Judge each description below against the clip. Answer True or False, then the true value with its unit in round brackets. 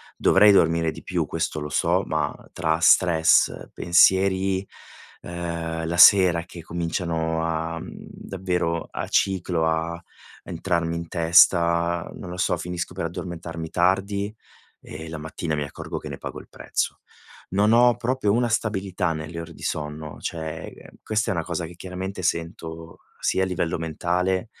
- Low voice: True (85 Hz)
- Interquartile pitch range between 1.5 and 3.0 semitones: True (2.4 semitones)